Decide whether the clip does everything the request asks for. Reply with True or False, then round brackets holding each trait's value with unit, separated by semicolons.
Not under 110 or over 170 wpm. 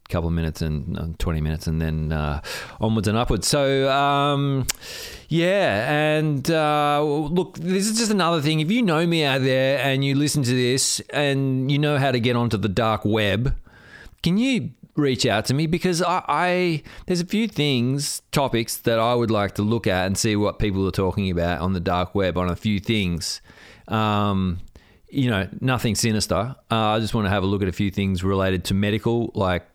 False (205 wpm)